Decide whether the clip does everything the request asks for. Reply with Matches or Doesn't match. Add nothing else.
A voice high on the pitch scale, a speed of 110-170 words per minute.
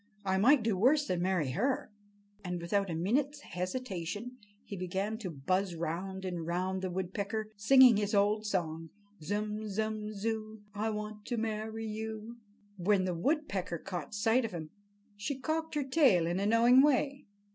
Matches